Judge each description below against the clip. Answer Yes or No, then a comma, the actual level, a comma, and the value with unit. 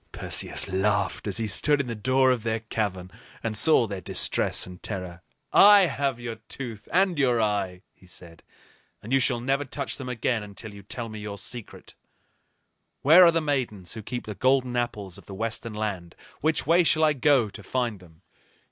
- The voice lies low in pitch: Yes, low, 115 Hz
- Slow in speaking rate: No, average, 190 wpm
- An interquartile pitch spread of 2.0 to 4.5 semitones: No, average, 4.9 semitones